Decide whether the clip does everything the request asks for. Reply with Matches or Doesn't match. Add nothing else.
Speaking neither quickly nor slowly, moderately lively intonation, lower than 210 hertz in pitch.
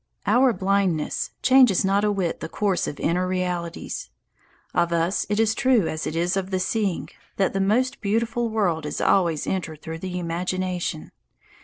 Matches